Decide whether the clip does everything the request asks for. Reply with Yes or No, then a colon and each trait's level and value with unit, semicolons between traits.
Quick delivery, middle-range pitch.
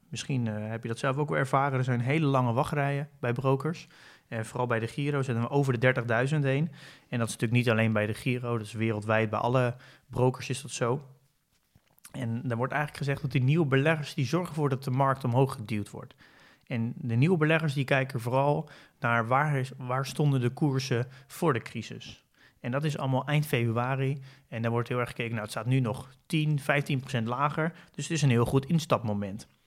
No: fast, 215 wpm; low, 130 Hz